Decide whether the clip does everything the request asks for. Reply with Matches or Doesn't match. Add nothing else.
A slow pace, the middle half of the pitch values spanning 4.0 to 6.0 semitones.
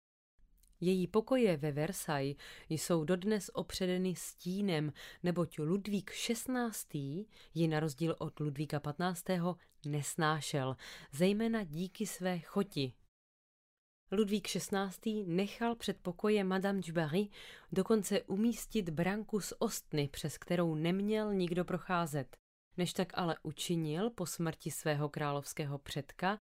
Matches